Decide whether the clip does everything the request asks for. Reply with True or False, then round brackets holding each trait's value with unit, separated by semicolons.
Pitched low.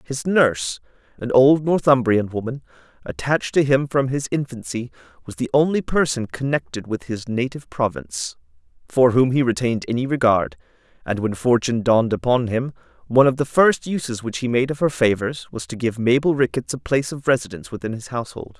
True (125 Hz)